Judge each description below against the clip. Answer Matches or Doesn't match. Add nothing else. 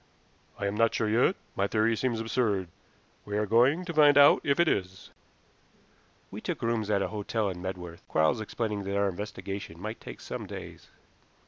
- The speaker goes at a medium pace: Matches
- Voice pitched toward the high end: Doesn't match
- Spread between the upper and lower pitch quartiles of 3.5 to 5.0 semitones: Doesn't match